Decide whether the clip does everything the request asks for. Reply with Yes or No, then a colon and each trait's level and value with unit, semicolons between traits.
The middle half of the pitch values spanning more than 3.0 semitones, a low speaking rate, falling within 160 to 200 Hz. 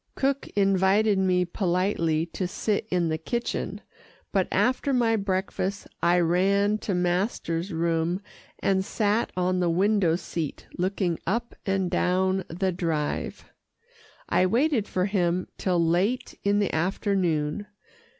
No: average, 2.7 semitones; slow, 130 wpm; medium, 185 Hz